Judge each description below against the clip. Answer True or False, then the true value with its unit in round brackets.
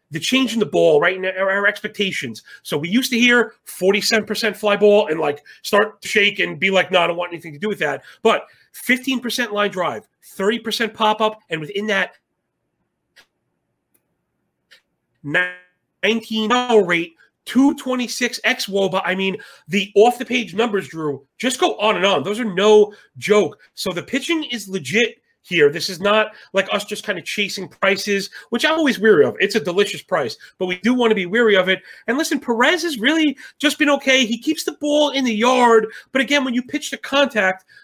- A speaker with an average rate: True (190 wpm)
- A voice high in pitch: True (215 Hz)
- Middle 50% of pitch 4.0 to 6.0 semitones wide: True (4.3 semitones)